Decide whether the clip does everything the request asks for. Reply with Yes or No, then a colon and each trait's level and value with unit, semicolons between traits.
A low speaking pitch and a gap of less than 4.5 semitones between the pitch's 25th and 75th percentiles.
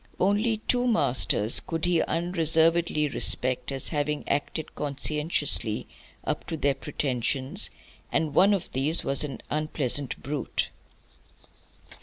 No: medium, 150 Hz; average, 3.3 semitones